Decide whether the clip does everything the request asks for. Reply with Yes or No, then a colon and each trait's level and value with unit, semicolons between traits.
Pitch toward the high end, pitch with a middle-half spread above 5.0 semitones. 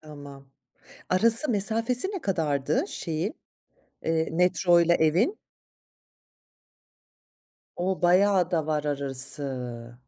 No: medium, 170 Hz; wide, 5.6 semitones